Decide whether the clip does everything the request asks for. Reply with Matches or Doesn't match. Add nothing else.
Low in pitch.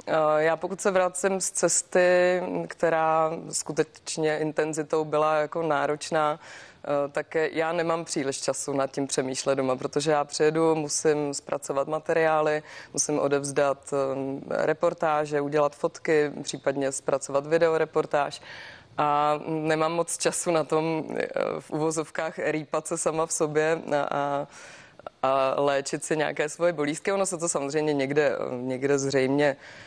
Doesn't match